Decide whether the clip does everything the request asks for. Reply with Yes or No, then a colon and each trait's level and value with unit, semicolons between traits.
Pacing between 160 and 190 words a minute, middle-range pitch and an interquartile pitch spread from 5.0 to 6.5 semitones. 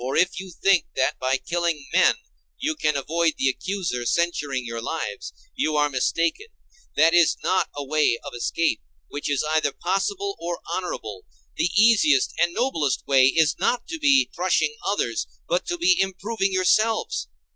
Yes: average, 165 wpm; medium, 170 Hz; wide, 5.4 semitones